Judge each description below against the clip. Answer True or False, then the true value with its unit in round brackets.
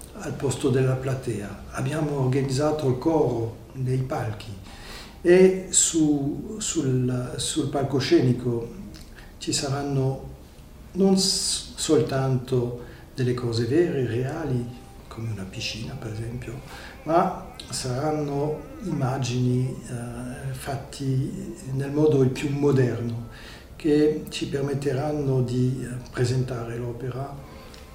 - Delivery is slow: True (95 wpm)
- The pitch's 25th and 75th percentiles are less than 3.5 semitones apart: True (3.0 semitones)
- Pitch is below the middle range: True (130 Hz)